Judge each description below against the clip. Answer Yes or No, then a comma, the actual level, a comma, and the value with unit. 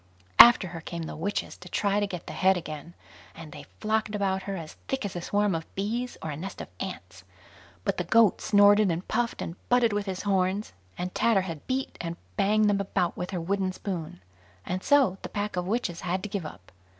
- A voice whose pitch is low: No, high, 190 Hz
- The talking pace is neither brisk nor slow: No, fast, 220 wpm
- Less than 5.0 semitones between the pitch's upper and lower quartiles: Yes, average, 3.1 semitones